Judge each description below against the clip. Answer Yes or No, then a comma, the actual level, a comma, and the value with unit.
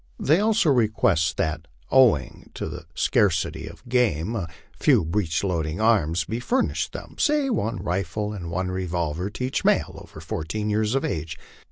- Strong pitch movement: Yes, wide, 6.1 semitones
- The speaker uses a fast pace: No, average, 165 wpm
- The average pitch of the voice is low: Yes, low, 100 Hz